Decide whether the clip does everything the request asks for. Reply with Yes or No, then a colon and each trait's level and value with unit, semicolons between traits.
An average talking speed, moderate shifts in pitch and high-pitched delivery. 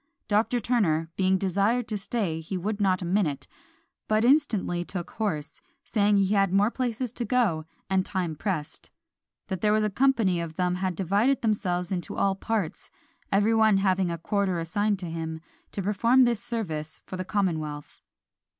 Yes: average, 175 wpm; average, 3.6 semitones; high, 195 Hz